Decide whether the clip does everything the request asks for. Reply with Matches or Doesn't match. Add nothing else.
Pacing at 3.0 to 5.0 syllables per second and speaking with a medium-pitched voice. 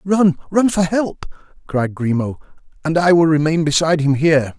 Doesn't match